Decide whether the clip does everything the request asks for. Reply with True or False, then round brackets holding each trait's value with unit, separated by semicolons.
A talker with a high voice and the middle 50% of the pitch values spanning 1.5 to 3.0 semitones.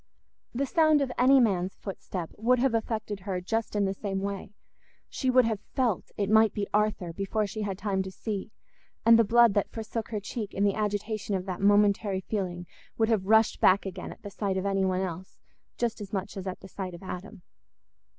True (205 Hz; 2.5 semitones)